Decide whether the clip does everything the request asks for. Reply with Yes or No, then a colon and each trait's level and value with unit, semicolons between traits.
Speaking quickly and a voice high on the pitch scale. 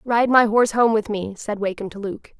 Yes: fast, 250 wpm; high, 215 Hz